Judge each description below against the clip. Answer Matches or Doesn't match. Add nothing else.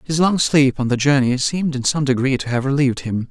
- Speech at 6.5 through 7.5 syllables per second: Doesn't match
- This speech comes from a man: Matches